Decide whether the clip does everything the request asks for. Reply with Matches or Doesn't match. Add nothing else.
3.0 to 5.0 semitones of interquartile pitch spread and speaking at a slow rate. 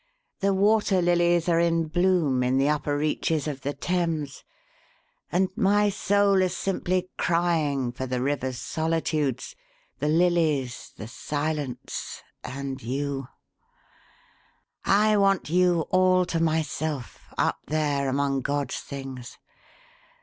Matches